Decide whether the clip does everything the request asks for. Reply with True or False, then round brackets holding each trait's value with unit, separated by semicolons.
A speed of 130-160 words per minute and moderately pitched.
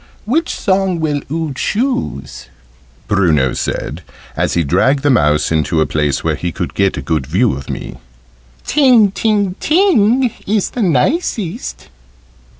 True (145 wpm; 155 Hz)